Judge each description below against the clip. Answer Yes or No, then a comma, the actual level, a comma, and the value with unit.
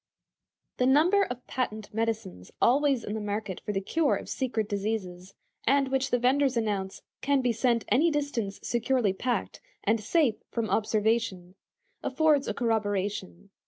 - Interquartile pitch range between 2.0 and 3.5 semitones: No, average, 4.4 semitones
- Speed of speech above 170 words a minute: No, average, 150 wpm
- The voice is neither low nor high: No, high, 230 Hz